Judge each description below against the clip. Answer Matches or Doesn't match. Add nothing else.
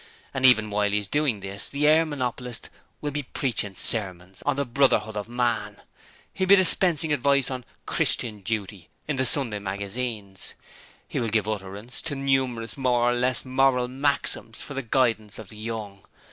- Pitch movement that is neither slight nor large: Matches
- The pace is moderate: Matches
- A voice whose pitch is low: Matches